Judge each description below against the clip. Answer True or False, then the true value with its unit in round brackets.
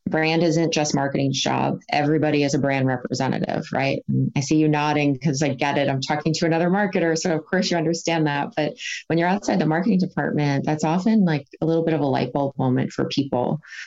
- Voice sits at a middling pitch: True (155 Hz)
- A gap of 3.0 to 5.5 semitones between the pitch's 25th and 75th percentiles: False (2.5 semitones)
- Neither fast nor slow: False (215 wpm)